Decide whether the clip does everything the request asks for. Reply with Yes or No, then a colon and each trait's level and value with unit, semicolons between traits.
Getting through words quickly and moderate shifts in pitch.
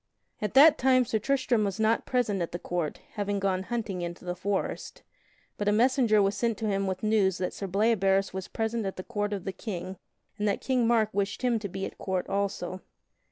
Yes: fast, 215 wpm; average, 3.0 semitones